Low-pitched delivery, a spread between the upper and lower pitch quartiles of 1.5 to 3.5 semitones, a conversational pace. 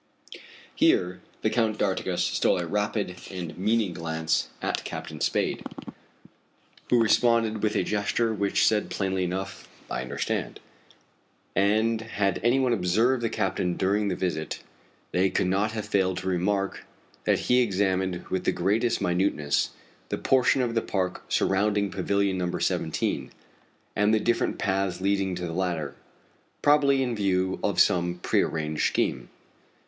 Yes: low, 100 Hz; average, 3.2 semitones; average, 145 wpm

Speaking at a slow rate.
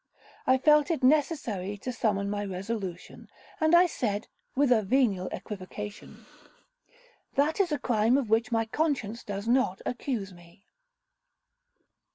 Yes: slow, 130 wpm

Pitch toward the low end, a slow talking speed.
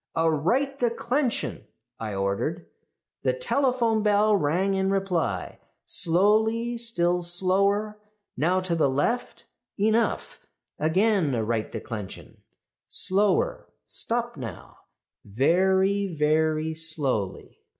No: high, 190 Hz; slow, 100 wpm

